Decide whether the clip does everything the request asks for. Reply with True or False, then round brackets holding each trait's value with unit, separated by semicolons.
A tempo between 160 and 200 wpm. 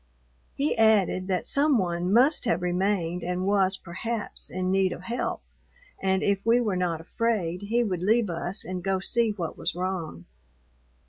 True (170 wpm)